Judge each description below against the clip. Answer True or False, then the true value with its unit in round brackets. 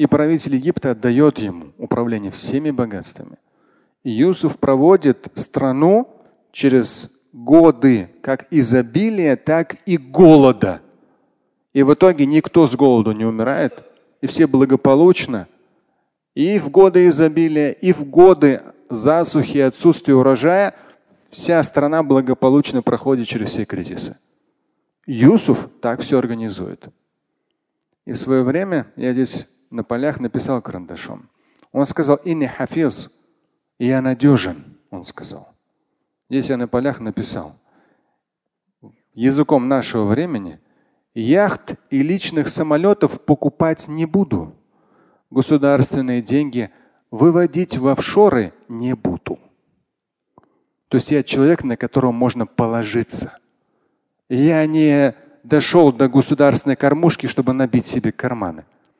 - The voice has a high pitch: False (140 Hz)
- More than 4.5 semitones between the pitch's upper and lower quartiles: False (4.0 semitones)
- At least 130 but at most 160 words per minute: False (110 wpm)